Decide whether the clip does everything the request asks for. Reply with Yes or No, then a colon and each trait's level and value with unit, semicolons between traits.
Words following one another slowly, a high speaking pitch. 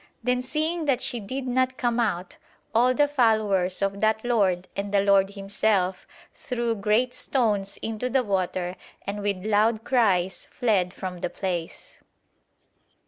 No: average, 145 wpm; high, 215 Hz